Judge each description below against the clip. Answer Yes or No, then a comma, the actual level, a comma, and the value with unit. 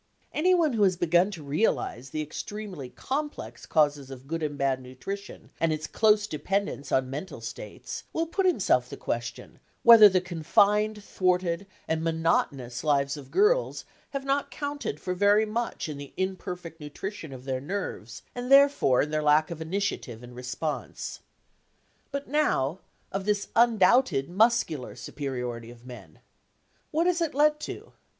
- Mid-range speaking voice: Yes, medium, 180 Hz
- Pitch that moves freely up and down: Yes, wide, 7.4 semitones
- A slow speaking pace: No, average, 155 wpm